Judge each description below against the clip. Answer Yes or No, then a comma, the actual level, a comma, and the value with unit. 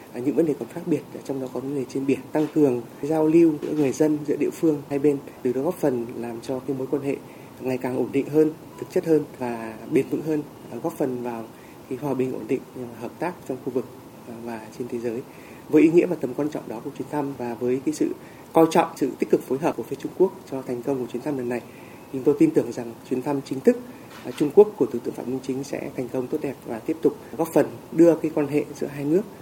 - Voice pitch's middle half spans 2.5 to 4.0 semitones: Yes, average, 3.7 semitones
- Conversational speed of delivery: No, fast, 270 wpm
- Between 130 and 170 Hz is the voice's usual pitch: Yes, medium, 140 Hz